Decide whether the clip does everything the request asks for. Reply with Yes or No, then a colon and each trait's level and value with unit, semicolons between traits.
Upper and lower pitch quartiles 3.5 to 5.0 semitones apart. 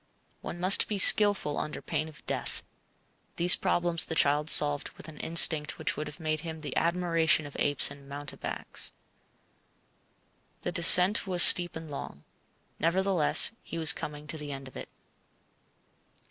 No: average, 2.9 semitones